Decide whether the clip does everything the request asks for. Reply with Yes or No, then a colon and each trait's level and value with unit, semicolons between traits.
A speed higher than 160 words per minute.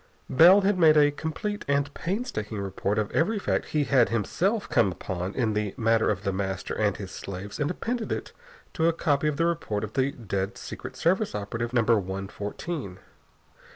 Yes: average, 190 wpm